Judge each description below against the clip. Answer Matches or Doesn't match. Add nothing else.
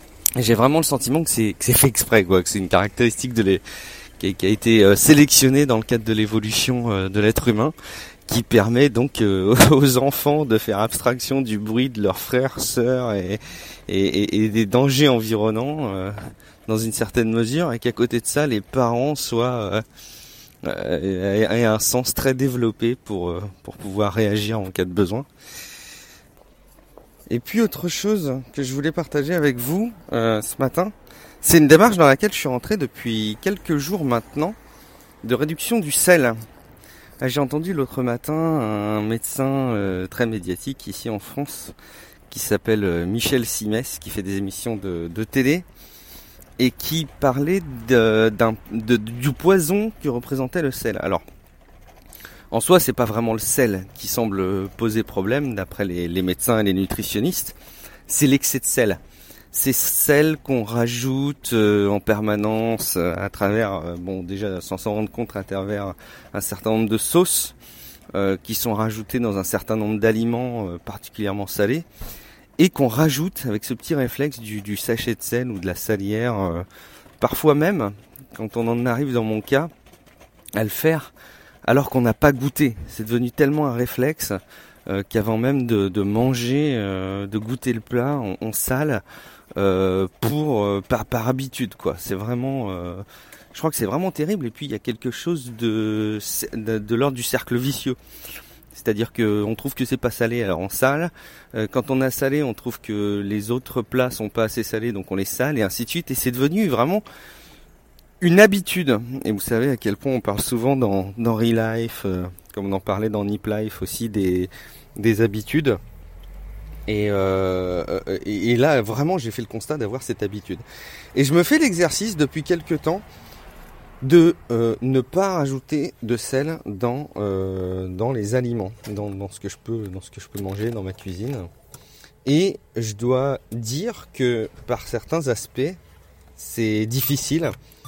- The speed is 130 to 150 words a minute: Doesn't match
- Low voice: Matches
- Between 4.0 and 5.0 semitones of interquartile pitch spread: Matches